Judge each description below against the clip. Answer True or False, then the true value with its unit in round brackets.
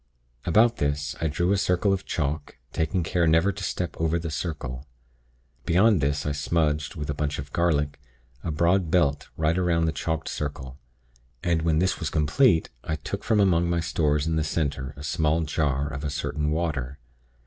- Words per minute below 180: False (185 wpm)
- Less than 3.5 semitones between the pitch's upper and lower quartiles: True (2.8 semitones)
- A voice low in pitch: True (80 Hz)